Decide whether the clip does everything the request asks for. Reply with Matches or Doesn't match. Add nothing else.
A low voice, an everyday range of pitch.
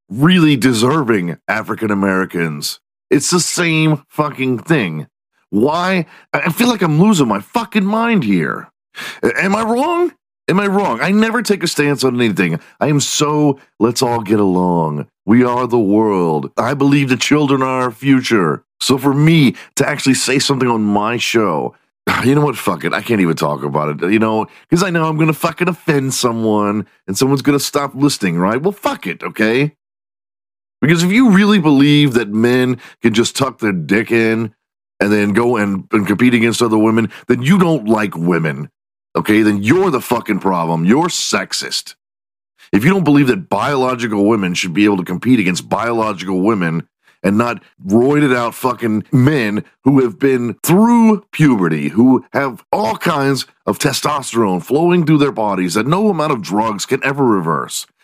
Doesn't match